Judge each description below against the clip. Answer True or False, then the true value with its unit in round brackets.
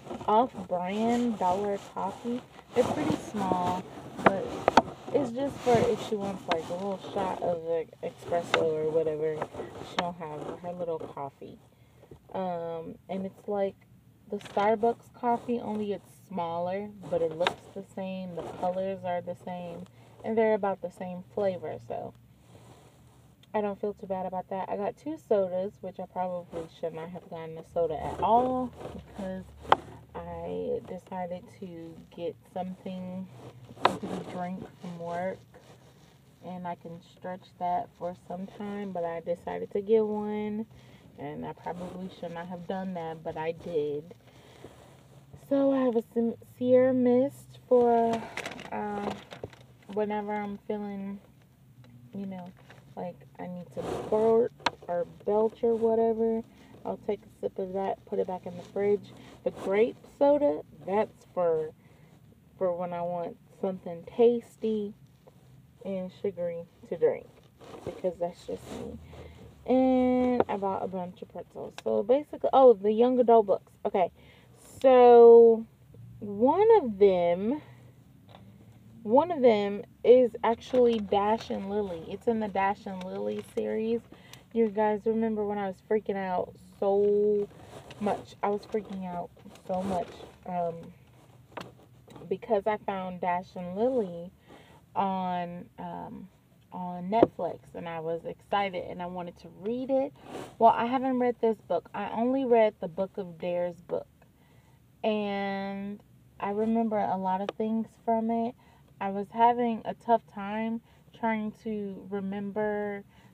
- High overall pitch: True (195 Hz)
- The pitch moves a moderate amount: True (4.5 semitones)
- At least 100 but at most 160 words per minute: True (140 wpm)